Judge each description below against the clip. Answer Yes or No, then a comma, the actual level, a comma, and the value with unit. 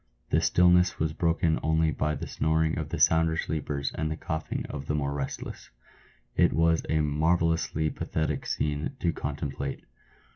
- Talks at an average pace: Yes, average, 155 wpm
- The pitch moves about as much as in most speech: No, narrow, 1.6 semitones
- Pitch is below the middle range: Yes, very low, 80 Hz